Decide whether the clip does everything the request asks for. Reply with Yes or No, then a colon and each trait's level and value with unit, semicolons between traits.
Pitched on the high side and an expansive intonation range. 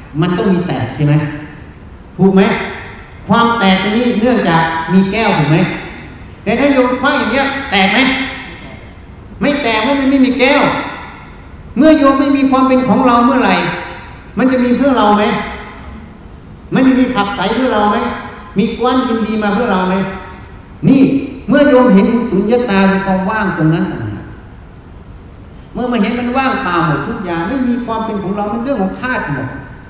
Yes: high, 215 Hz; wide, 5.9 semitones